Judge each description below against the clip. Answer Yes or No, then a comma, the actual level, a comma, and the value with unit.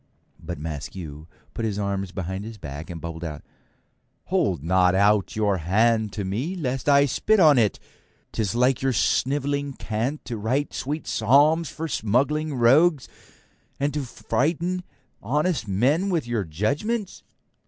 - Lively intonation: Yes, wide, 6.9 semitones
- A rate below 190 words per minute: Yes, average, 150 wpm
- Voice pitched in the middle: No, low, 120 Hz